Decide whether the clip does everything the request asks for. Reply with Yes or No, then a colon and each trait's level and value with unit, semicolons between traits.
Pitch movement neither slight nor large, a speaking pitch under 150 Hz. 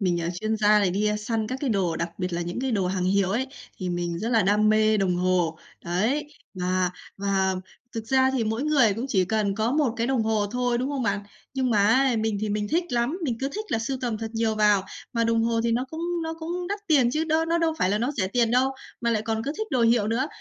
No: average, 4.3 semitones; high, 225 Hz